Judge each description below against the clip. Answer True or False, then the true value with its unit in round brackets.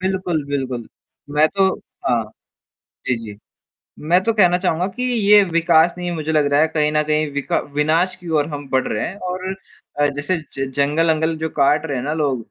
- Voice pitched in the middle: True (155 Hz)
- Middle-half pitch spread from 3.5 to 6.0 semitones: True (3.8 semitones)